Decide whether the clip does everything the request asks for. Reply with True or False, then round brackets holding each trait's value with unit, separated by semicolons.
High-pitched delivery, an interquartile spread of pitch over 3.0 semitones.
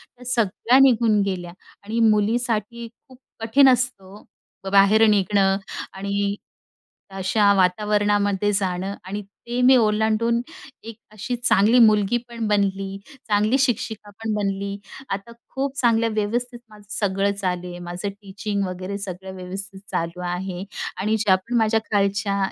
False (205 Hz; 2.6 semitones)